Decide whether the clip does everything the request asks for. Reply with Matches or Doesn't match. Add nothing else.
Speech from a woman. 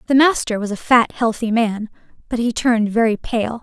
Matches